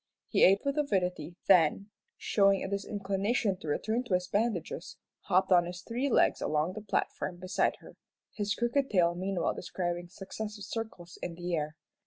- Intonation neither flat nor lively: Yes, average, 3.3 semitones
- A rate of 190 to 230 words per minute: No, average, 165 wpm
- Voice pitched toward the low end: No, high, 190 Hz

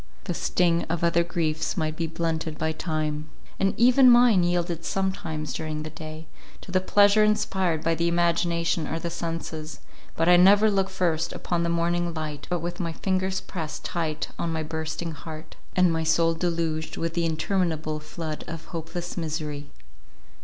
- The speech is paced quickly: No, average, 170 wpm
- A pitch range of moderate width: No, narrow, 2.0 semitones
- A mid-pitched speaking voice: Yes, medium, 165 Hz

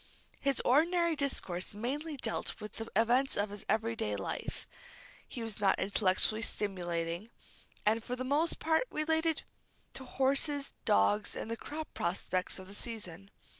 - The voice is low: No, high, 225 Hz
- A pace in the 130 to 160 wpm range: Yes, average, 145 wpm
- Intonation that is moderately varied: No, wide, 6.0 semitones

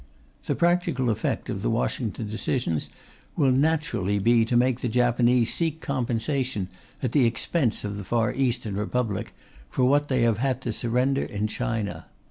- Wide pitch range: No, average, 3.2 semitones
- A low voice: Yes, low, 120 Hz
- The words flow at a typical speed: Yes, average, 160 wpm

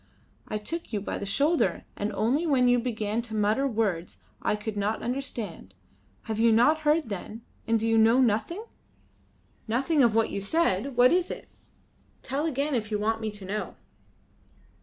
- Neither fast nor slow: Yes, average, 175 wpm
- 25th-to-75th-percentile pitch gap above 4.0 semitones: Yes, average, 4.5 semitones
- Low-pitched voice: No, high, 225 Hz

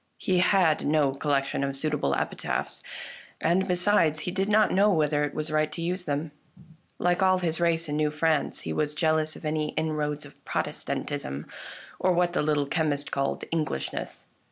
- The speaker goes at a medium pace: Yes, average, 180 wpm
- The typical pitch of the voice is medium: Yes, medium, 155 Hz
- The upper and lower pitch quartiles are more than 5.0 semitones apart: No, average, 3.0 semitones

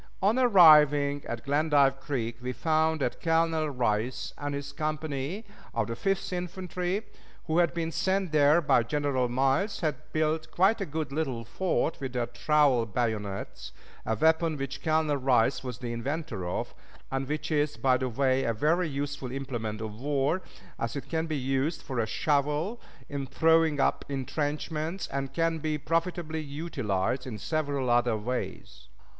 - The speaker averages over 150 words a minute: Yes, average, 160 wpm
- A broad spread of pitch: No, average, 3.9 semitones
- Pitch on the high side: No, medium, 145 Hz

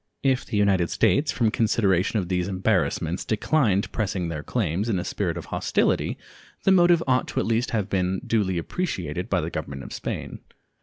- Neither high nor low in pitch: No, low, 100 Hz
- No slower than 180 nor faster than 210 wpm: Yes, average, 185 wpm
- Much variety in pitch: No, average, 4.5 semitones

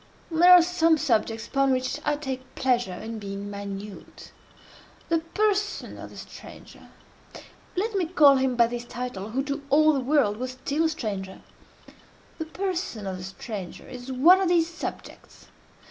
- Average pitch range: No, wide, 6.6 semitones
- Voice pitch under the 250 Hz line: No, very high, 265 Hz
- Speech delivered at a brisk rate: No, average, 155 wpm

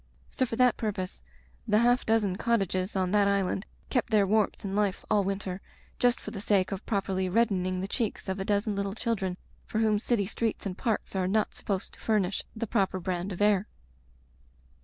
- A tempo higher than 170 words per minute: Yes, average, 195 wpm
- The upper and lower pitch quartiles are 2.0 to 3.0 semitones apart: Yes, narrow, 2.5 semitones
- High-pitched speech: Yes, high, 200 Hz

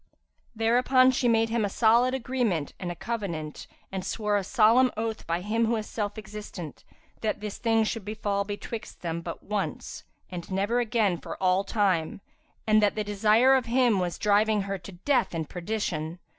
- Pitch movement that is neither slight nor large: Yes, average, 3.2 semitones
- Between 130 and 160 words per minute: No, average, 180 wpm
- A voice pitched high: Yes, high, 210 Hz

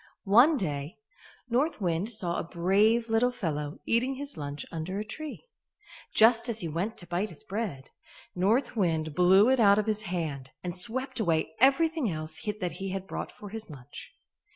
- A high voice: Yes, high, 195 Hz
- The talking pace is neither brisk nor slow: Yes, average, 175 wpm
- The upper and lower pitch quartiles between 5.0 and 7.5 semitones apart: Yes, wide, 5.6 semitones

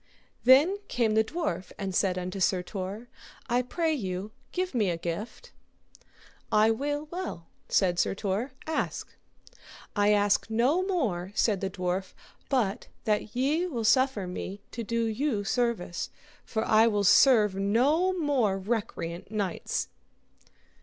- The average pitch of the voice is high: Yes, high, 220 Hz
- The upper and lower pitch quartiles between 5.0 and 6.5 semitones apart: Yes, average, 5.3 semitones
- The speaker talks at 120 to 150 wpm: Yes, average, 140 wpm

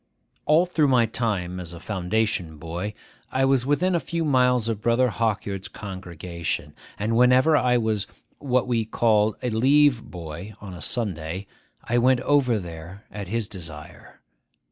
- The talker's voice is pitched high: No, low, 110 Hz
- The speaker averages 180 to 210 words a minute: No, average, 155 wpm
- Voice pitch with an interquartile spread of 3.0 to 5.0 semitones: No, wide, 5.4 semitones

